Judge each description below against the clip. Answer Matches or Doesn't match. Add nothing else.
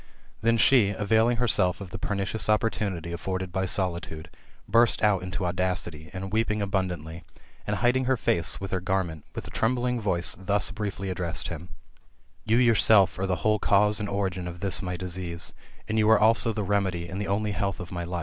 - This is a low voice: Matches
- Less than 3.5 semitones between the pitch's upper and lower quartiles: Matches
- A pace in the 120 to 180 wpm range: Doesn't match